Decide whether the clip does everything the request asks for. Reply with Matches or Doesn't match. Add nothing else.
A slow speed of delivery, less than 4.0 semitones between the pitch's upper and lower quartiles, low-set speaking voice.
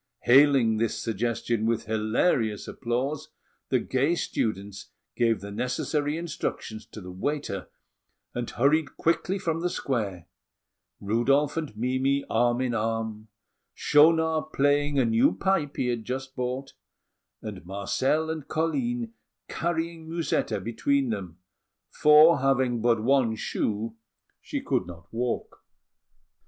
Doesn't match